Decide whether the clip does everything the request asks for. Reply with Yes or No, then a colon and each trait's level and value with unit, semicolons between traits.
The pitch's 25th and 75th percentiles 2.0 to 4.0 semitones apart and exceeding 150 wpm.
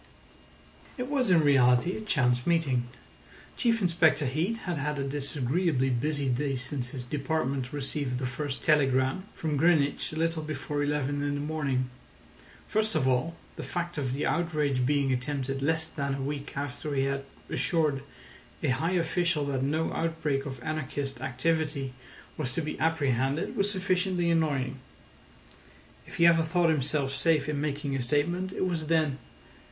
Yes: average, 3.4 semitones; average, 160 wpm